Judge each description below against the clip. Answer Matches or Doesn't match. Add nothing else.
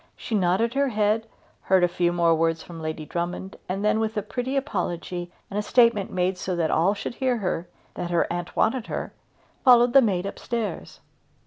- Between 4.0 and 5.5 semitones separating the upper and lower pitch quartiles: Matches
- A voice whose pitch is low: Doesn't match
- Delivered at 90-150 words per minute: Doesn't match